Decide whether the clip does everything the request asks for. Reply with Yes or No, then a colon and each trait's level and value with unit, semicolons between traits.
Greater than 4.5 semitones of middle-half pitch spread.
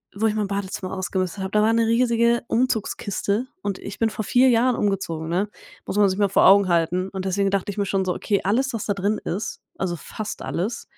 No: average, 2.8 semitones